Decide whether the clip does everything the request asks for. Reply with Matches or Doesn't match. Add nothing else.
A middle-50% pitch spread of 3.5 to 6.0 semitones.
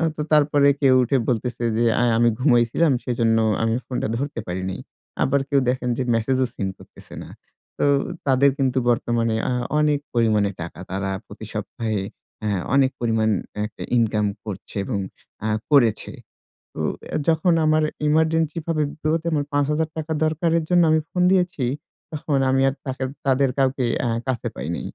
Matches